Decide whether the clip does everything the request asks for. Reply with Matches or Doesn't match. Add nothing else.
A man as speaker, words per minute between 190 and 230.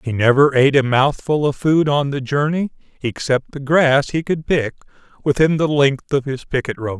Matches